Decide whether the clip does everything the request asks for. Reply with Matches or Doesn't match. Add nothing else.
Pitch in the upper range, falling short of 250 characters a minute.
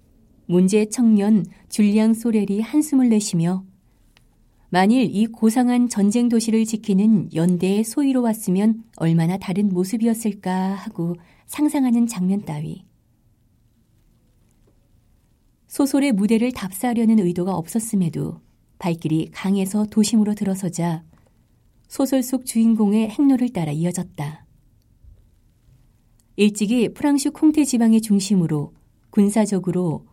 Doesn't match